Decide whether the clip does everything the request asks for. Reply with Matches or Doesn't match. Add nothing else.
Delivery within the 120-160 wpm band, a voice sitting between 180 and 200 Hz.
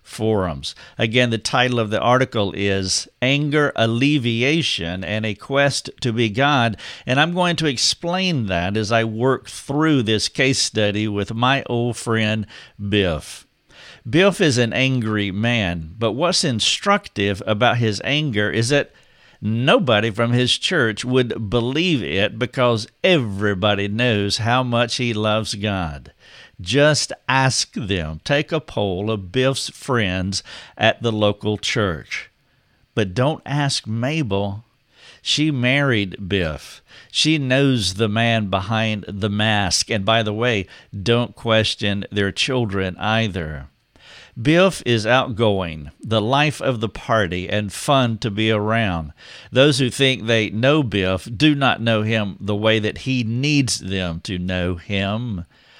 Doesn't match